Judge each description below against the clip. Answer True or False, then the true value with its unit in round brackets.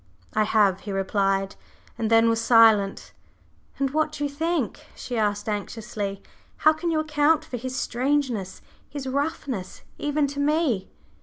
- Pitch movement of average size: False (5.9 semitones)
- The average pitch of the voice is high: True (245 Hz)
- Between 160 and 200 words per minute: False (150 wpm)